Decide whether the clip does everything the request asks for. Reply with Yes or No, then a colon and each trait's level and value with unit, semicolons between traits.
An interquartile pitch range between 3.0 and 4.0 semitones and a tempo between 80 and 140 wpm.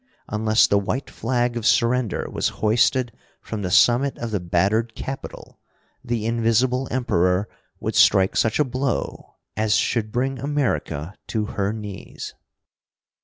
Yes: average, 3.4 semitones; slow, 135 wpm